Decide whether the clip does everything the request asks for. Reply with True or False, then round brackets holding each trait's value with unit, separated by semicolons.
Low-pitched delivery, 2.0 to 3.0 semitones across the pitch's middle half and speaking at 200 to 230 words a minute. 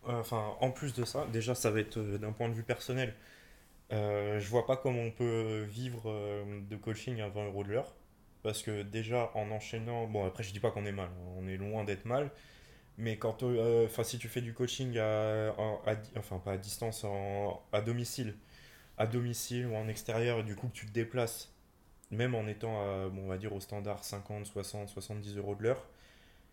True (110 Hz; 2.4 semitones; 215 wpm)